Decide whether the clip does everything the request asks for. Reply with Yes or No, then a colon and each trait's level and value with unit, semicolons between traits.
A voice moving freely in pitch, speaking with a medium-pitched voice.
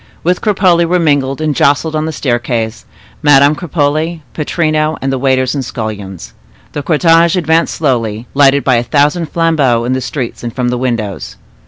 No: average, 4.3 semitones; medium, 145 Hz